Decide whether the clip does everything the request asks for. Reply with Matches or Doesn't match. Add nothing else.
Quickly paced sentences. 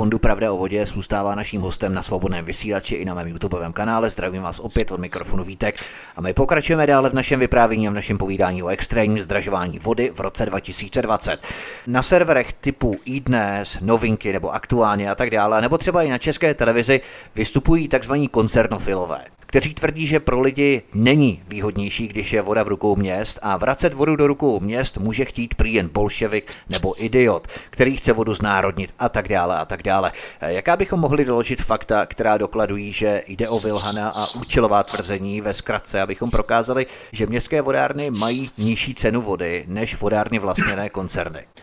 Matches